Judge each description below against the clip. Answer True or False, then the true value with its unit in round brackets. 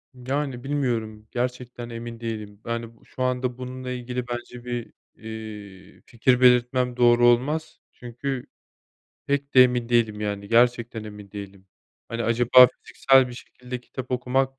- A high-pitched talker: False (120 Hz)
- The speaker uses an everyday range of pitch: False (1.8 semitones)